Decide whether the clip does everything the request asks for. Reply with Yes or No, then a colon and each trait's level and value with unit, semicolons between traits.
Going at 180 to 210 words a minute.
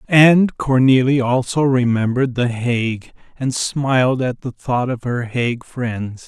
No: average, 145 wpm